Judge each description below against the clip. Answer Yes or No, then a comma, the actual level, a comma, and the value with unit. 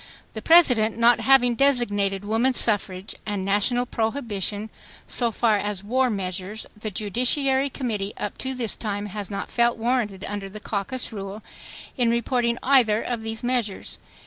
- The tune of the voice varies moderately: Yes, average, 3.2 semitones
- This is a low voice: No, high, 220 Hz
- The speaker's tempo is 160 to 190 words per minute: No, average, 150 wpm